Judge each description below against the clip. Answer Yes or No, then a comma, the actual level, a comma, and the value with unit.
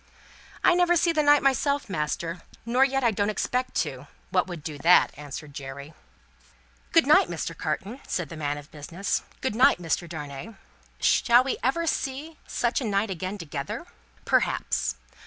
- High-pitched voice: Yes, high, 200 Hz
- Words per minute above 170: No, average, 165 wpm